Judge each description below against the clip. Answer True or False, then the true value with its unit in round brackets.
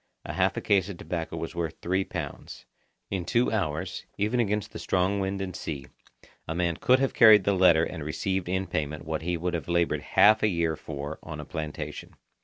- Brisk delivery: True (210 wpm)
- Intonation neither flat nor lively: True (3.5 semitones)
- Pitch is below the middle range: True (90 Hz)